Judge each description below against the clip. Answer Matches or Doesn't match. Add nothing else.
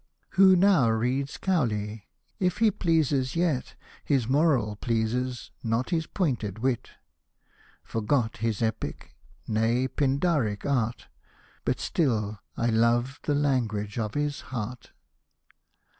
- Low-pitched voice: Matches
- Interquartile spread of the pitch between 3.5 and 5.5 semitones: Matches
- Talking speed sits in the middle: Doesn't match